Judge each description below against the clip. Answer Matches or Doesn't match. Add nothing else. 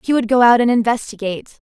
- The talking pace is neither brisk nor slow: Doesn't match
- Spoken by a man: Doesn't match